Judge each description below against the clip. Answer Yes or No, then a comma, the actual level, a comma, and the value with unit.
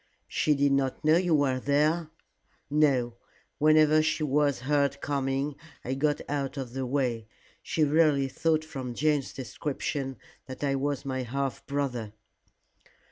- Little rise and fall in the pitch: Yes, narrow, 2.2 semitones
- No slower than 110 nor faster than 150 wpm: Yes, average, 140 wpm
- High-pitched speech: No, medium, 140 Hz